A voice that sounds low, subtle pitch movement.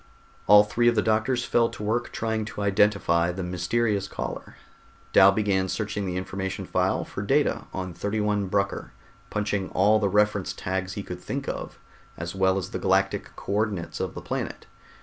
Yes: low, 100 Hz; narrow, 2.2 semitones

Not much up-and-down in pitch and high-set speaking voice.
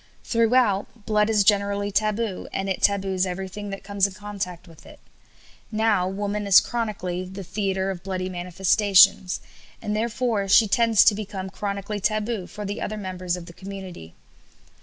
Yes: narrow, 1.9 semitones; high, 200 Hz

